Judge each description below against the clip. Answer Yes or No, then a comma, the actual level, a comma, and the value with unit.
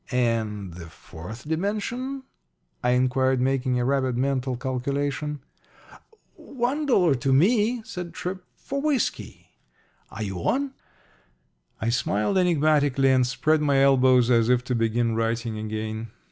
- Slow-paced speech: Yes, slow, 130 wpm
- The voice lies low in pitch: Yes, low, 130 Hz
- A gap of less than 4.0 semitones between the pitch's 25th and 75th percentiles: No, wide, 5.5 semitones